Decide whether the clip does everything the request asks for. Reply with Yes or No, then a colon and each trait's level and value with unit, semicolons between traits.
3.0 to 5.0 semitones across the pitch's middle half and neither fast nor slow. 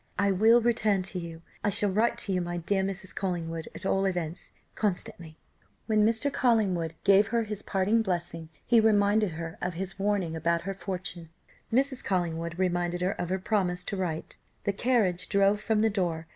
Yes: average, 3.3 semitones; average, 185 wpm